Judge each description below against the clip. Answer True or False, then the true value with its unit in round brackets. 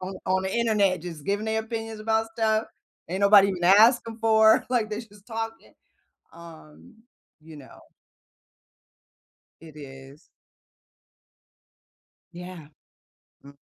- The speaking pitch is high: True (200 Hz)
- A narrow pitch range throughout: False (4.6 semitones)